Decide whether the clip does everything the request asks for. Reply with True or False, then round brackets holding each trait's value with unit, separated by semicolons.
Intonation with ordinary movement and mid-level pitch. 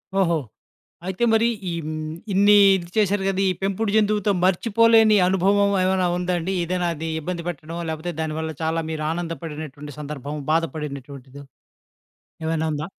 True (3.8 semitones; 170 Hz)